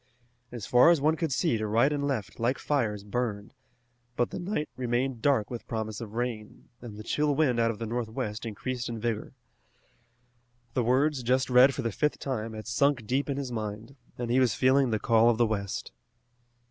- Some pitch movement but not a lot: Yes, average, 3.3 semitones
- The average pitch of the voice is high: No, low, 120 Hz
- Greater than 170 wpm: Yes, average, 200 wpm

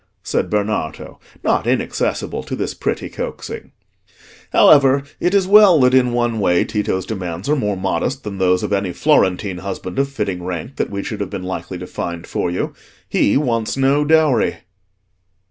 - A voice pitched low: Yes, low, 105 Hz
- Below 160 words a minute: No, average, 170 wpm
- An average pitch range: No, wide, 6.6 semitones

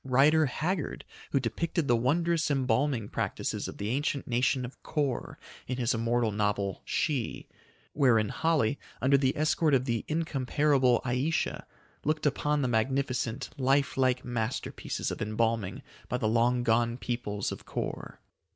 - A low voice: Yes, low, 130 Hz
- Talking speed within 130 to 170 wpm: Yes, average, 140 wpm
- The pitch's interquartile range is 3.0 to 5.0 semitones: Yes, average, 3.7 semitones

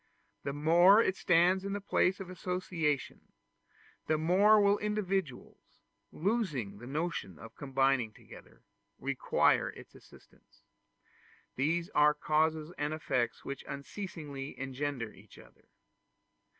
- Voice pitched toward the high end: No, medium, 155 Hz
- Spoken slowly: Yes, slow, 115 wpm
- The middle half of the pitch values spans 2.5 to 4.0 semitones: No, average, 5.3 semitones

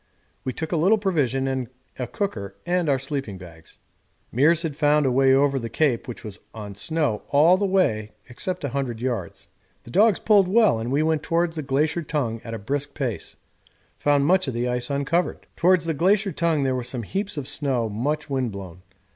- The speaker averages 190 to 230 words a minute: Yes, fast, 205 wpm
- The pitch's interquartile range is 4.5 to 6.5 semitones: Yes, wide, 5.4 semitones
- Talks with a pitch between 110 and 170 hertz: Yes, medium, 140 Hz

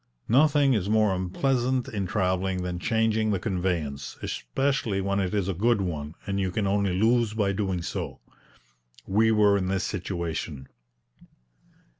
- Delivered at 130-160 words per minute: Yes, average, 150 wpm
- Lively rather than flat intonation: No, average, 3.2 semitones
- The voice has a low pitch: Yes, low, 100 Hz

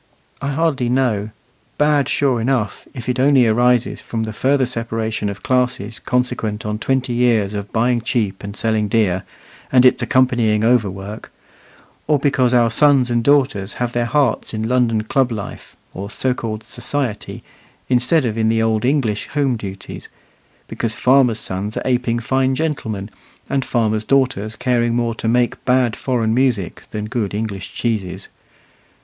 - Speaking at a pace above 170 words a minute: No, average, 155 wpm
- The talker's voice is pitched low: Yes, low, 120 Hz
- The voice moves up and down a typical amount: Yes, average, 3.0 semitones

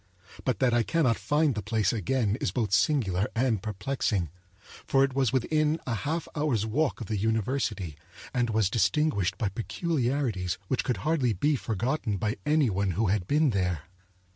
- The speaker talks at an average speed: Yes, average, 170 wpm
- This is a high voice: No, low, 115 Hz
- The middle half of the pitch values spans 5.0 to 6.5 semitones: Yes, average, 5.3 semitones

